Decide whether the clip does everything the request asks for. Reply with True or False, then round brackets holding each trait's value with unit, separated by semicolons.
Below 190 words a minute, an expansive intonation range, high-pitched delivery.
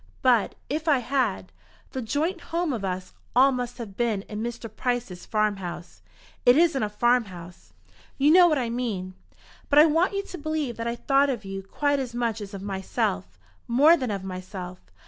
False (195 wpm; 6.2 semitones; 240 Hz)